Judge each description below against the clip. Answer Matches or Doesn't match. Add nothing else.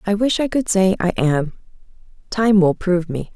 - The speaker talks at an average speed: Matches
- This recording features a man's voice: Doesn't match